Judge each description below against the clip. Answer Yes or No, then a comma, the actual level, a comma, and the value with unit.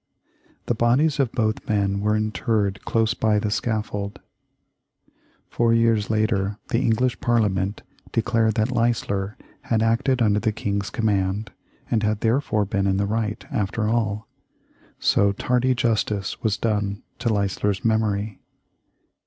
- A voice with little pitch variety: Yes, narrow, 2.2 semitones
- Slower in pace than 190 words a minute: Yes, slow, 135 wpm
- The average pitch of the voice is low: Yes, low, 110 Hz